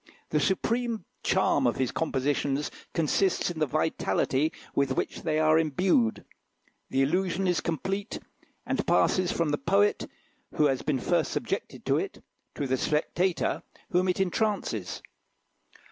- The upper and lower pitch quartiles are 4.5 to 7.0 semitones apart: Yes, average, 5.0 semitones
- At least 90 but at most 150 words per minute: Yes, average, 140 wpm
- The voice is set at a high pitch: No, medium, 160 Hz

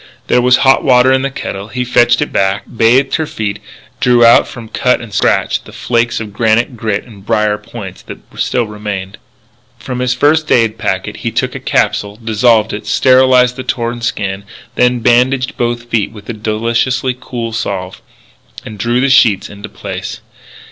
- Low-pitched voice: Yes, low, 115 Hz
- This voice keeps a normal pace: Yes, average, 180 wpm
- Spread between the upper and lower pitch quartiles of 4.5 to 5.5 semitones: No, average, 2.8 semitones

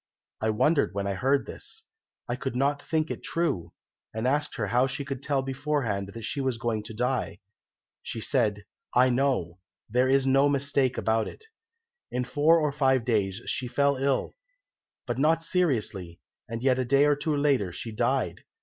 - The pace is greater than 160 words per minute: Yes, average, 180 wpm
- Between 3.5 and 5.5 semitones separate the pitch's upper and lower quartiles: Yes, average, 3.9 semitones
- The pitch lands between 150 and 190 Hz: No, low, 130 Hz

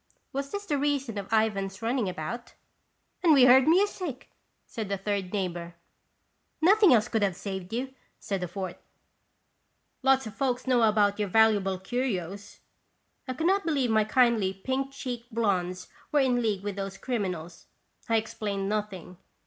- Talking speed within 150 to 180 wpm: Yes, average, 165 wpm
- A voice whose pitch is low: No, high, 220 Hz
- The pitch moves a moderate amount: Yes, average, 5.0 semitones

